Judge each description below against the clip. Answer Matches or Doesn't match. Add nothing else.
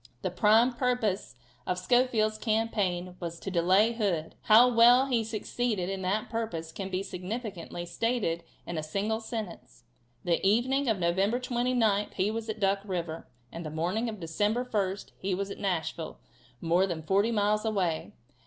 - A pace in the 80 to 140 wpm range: Doesn't match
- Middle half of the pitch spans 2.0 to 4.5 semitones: Matches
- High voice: Matches